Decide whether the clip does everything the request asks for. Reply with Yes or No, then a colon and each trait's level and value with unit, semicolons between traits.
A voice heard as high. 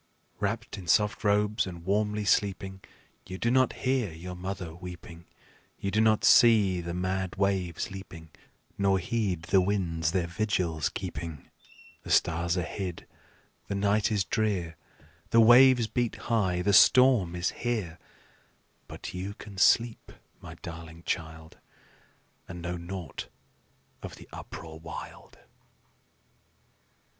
No: very low, 95 Hz